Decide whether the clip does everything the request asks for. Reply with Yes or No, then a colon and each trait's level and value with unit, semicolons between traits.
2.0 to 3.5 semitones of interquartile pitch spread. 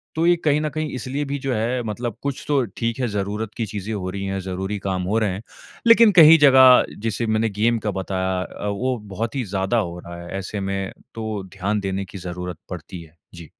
No: average, 4.8 semitones